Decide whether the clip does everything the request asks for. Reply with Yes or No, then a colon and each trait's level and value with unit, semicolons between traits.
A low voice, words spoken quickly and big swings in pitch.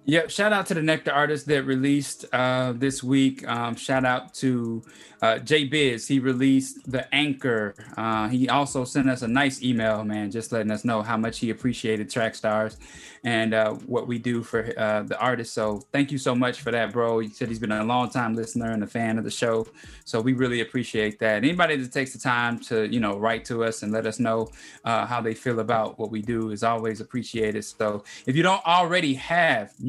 No: low, 120 Hz; fast, 220 wpm; average, 3.0 semitones